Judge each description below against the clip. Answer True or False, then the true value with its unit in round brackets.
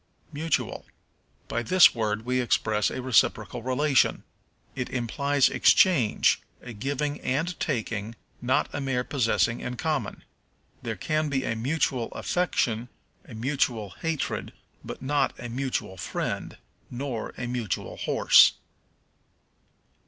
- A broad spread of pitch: False (3.7 semitones)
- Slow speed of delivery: True (125 wpm)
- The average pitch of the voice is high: False (125 Hz)